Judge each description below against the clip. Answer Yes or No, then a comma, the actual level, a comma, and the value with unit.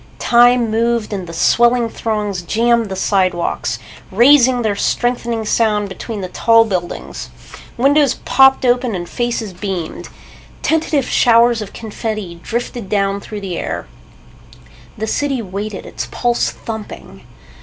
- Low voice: No, high, 225 Hz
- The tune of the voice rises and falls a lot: No, average, 3.3 semitones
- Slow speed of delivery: Yes, slow, 130 wpm